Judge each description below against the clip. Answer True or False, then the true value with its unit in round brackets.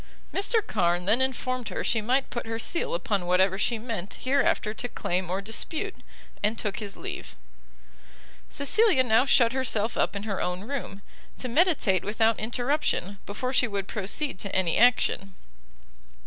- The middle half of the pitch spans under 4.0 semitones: False (4.7 semitones)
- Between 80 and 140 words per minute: False (160 wpm)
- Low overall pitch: False (225 Hz)